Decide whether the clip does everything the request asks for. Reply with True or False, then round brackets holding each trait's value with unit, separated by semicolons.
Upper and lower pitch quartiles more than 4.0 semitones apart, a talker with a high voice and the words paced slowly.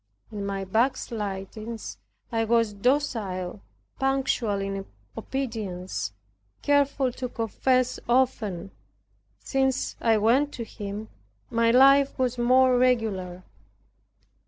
True (4.4 semitones; 230 Hz; 95 wpm)